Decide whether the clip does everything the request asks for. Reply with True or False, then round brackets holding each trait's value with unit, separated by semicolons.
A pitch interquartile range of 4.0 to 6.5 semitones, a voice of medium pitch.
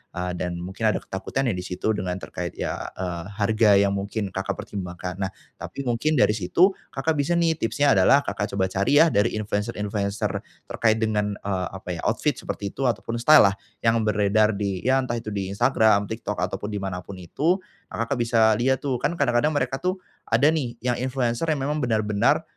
False (4.5 semitones; 110 Hz)